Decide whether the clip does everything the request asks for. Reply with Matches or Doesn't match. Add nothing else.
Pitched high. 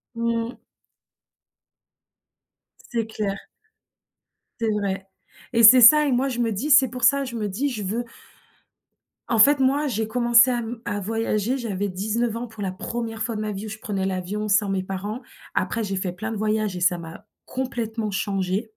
Matches